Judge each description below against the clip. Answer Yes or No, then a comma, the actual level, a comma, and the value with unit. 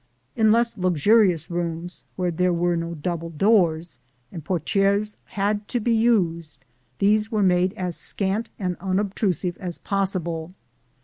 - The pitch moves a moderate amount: Yes, average, 3.4 semitones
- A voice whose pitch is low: No, medium, 185 Hz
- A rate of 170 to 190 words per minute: No, slow, 135 wpm